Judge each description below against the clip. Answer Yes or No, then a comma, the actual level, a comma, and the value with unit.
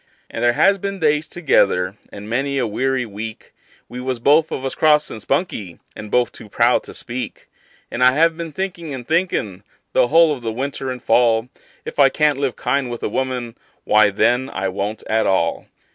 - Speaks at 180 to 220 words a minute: Yes, average, 200 wpm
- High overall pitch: No, low, 125 Hz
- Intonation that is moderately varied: Yes, average, 4.9 semitones